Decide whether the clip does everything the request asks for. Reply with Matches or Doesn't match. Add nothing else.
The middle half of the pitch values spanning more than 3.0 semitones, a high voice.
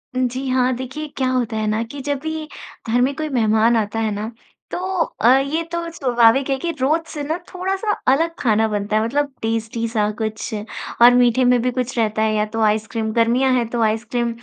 Matches